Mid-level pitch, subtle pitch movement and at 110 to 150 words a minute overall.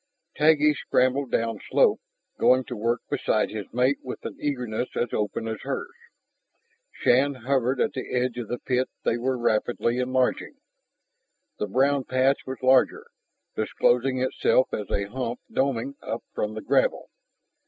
No: low, 125 Hz; narrow, 2.2 semitones; average, 145 wpm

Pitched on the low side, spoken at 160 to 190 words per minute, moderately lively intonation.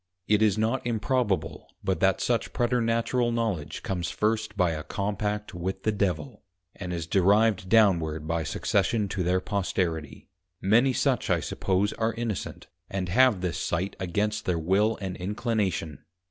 No: low, 100 Hz; average, 150 wpm; average, 3.7 semitones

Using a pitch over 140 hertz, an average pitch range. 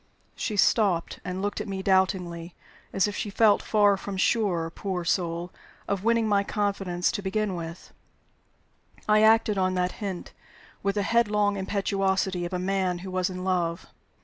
No: high, 190 Hz; narrow, 2.2 semitones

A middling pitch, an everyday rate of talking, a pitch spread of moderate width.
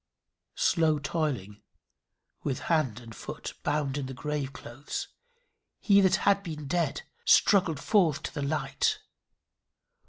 No: medium, 150 Hz; slow, 125 wpm; average, 3.8 semitones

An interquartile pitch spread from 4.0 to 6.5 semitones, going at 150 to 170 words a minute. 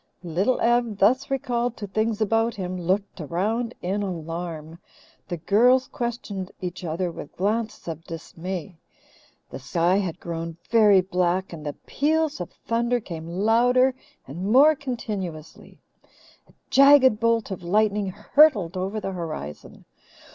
No: average, 5.2 semitones; slow, 135 wpm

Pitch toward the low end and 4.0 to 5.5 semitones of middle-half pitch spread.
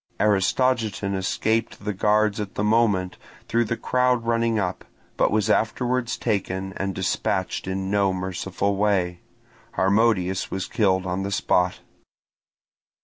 No: low, 100 Hz; average, 2.9 semitones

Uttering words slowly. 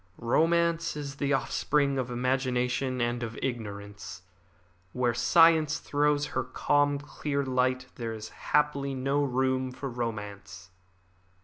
Yes: slow, 120 wpm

